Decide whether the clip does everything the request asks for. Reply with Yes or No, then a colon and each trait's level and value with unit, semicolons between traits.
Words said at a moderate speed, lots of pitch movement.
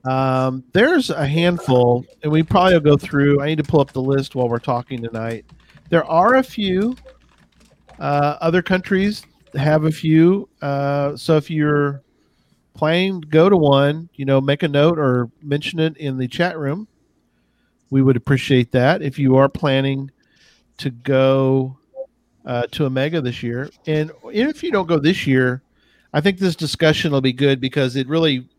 No: average, 175 wpm; average, 3.6 semitones